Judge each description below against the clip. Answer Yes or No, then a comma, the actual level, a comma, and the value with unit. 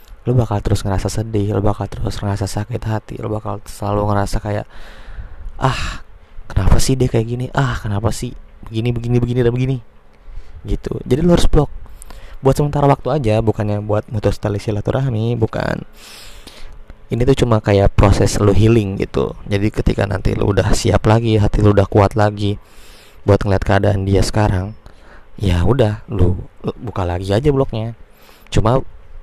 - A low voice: Yes, low, 105 Hz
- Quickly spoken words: Yes, fast, 160 wpm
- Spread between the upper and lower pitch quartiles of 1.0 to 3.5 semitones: Yes, average, 2.9 semitones